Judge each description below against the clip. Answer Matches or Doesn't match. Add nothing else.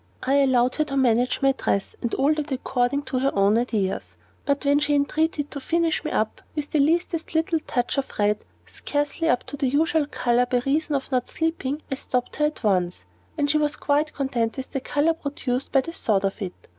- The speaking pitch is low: Doesn't match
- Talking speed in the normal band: Doesn't match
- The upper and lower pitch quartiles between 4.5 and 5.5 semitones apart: Doesn't match